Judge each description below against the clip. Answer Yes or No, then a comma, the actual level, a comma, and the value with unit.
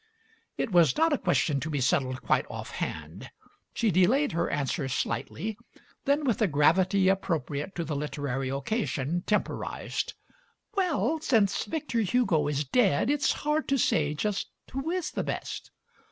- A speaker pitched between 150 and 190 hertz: Yes, medium, 185 Hz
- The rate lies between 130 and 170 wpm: Yes, average, 150 wpm